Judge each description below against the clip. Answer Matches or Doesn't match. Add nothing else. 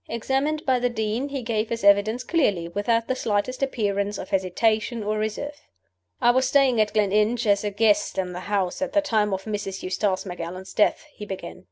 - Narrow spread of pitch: Doesn't match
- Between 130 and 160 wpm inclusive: Doesn't match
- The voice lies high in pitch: Matches